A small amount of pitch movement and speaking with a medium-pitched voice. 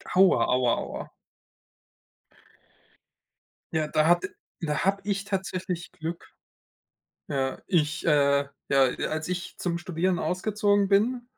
No: average, 4.2 semitones; medium, 175 Hz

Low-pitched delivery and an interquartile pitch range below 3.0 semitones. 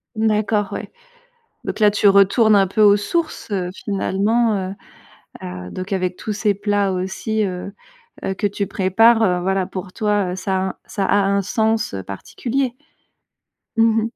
No: high, 200 Hz; narrow, 2.5 semitones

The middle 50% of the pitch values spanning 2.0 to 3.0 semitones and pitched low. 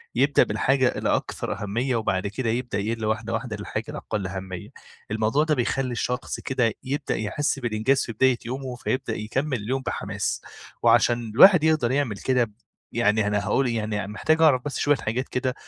No: average, 3.6 semitones; low, 120 Hz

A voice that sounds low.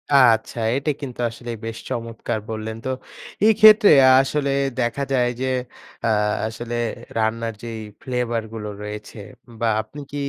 Yes: low, 115 Hz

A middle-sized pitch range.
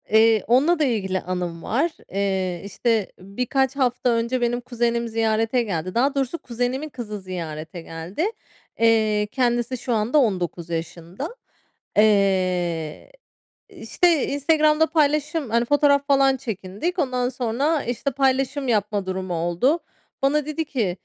No: wide, 6.1 semitones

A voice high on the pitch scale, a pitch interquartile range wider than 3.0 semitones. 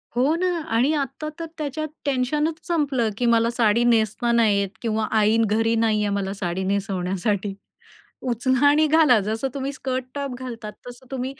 Yes: high, 235 Hz; average, 4.2 semitones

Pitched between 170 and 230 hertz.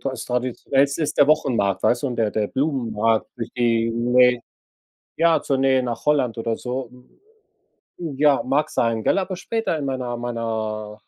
No: low, 125 Hz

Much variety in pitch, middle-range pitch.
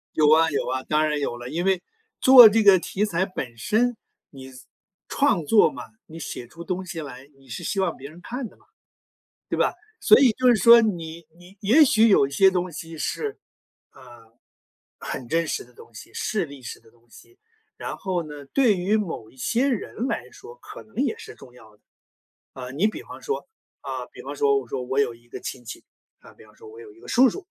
Yes: wide, 8.9 semitones; medium, 175 Hz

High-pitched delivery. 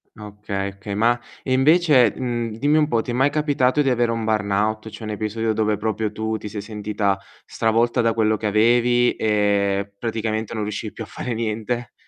No: low, 110 Hz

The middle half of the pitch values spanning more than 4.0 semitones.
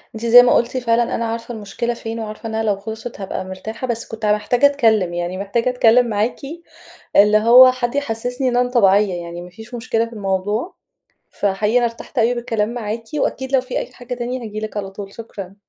No: average, 2.8 semitones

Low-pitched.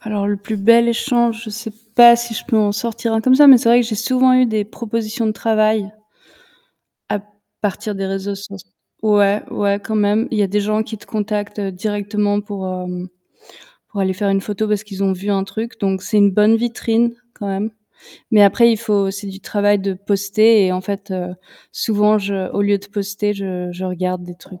No: high, 205 Hz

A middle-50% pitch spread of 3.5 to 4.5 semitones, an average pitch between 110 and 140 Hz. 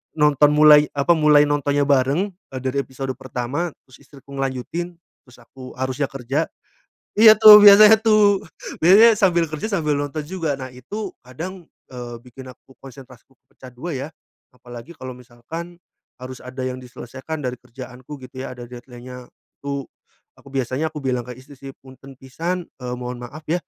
Yes: average, 3.9 semitones; low, 135 Hz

